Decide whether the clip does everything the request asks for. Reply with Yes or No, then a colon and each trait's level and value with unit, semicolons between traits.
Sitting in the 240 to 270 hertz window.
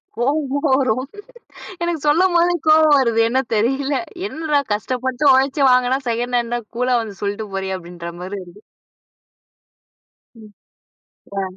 Yes: very high, 250 Hz